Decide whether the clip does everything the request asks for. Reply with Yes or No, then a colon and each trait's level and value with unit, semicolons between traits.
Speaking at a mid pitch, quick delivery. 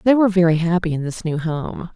Yes: medium, 175 Hz; fast, 245 wpm